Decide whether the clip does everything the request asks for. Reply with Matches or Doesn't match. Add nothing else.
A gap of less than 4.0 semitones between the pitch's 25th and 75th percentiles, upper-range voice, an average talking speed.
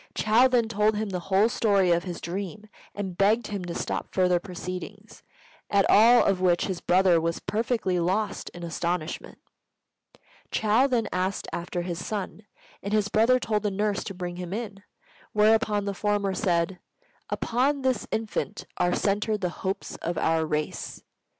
Matches